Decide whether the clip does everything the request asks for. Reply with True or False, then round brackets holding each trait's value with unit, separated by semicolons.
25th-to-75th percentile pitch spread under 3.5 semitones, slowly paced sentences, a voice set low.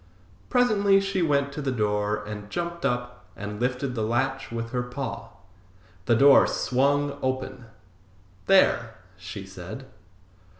False (4.2 semitones; 130 wpm; 125 Hz)